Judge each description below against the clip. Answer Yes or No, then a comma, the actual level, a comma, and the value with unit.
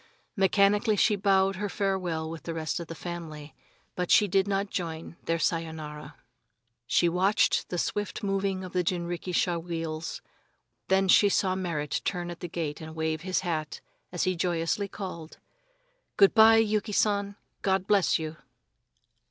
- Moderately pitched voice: Yes, medium, 180 Hz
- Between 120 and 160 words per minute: Yes, average, 155 wpm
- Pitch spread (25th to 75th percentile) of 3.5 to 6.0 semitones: No, average, 3.1 semitones